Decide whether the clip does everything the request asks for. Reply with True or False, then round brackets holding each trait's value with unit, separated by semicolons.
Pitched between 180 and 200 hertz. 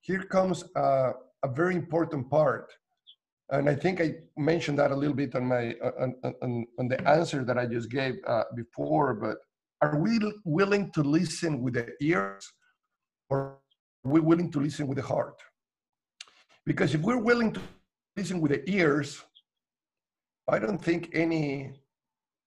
False (145 Hz)